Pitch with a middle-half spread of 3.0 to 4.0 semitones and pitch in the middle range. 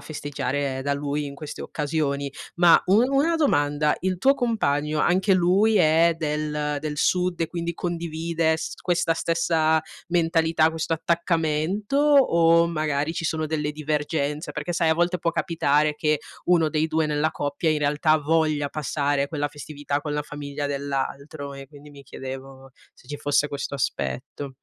No: narrow, 2.5 semitones; medium, 155 Hz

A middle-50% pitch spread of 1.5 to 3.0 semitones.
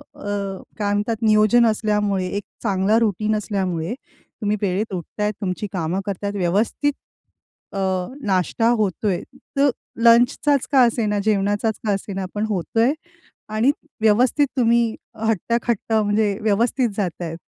Yes: narrow, 2.5 semitones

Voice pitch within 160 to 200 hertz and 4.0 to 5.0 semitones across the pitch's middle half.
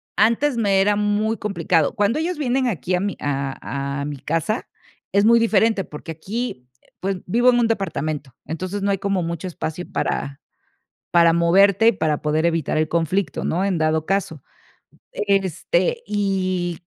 Yes: high, 190 Hz; average, 4.7 semitones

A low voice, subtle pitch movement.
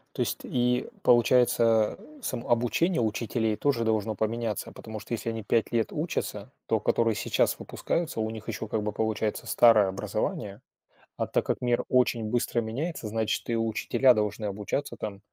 Yes: low, 115 Hz; narrow, 2.0 semitones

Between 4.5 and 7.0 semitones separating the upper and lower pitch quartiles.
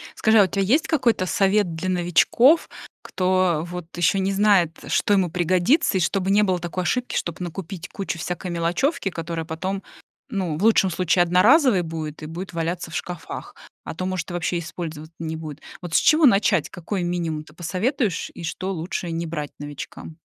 No: average, 2.9 semitones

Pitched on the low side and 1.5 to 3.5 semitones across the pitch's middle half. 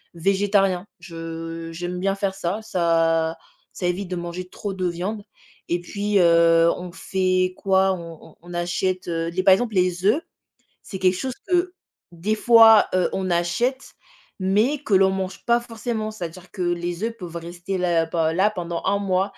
No: medium, 185 Hz; average, 2.8 semitones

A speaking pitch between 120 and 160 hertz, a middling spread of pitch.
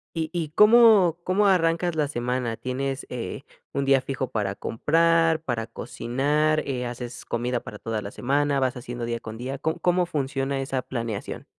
Yes: low, 135 Hz; average, 4.7 semitones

